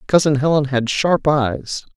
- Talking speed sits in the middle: Yes, average, 155 wpm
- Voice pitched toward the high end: No, medium, 140 Hz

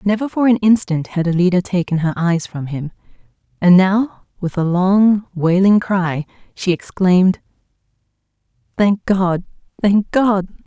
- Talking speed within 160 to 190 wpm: No, slow, 135 wpm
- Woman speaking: Yes, female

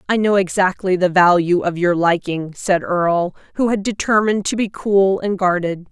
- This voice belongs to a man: No, female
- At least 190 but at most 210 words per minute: No, average, 180 wpm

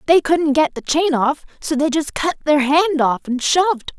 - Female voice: Yes, female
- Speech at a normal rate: No, fast, 225 wpm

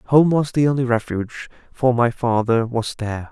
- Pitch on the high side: No, low, 125 Hz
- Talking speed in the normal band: Yes, average, 180 wpm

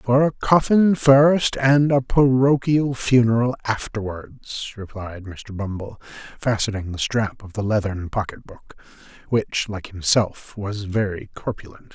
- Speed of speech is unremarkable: No, slow, 130 wpm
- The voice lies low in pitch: Yes, low, 115 Hz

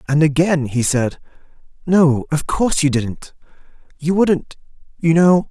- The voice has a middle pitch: Yes, medium, 155 Hz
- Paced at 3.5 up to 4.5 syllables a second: Yes, 4.2 syllables/s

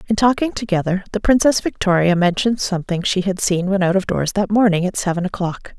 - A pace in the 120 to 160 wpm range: No, fast, 205 wpm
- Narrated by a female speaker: Yes, female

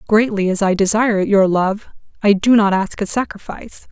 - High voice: Yes, high, 205 Hz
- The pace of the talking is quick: No, average, 185 wpm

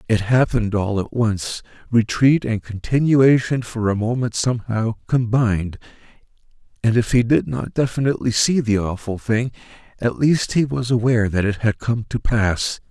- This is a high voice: No, low, 115 Hz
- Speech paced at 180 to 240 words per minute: No, average, 160 wpm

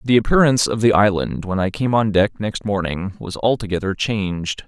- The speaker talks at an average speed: Yes, average, 195 wpm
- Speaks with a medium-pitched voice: No, low, 105 Hz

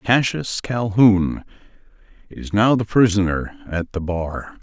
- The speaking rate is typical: No, slow, 115 wpm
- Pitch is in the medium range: No, low, 110 Hz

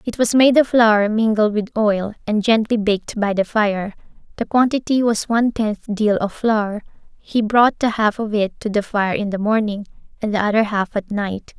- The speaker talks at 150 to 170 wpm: No, fast, 205 wpm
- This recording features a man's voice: No, female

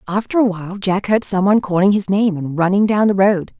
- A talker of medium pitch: No, high, 195 Hz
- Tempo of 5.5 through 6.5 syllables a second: Yes, 5.9 syllables/s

